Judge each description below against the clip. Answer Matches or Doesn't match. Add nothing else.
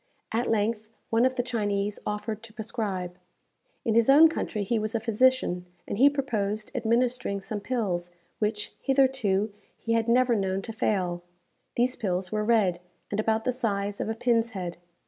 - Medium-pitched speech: Doesn't match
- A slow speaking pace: Doesn't match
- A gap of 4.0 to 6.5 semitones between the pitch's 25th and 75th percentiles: Doesn't match